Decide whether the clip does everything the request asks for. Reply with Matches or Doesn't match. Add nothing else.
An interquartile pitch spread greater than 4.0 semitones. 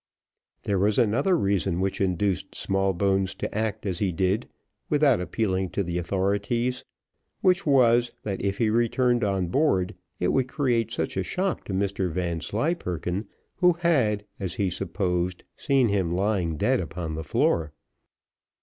Matches